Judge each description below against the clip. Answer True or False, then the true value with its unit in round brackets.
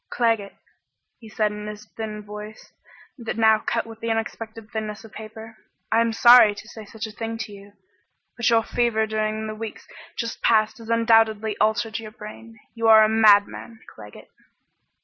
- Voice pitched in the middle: False (220 Hz)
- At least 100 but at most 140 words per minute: False (175 wpm)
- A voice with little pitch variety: True (1.0 semitones)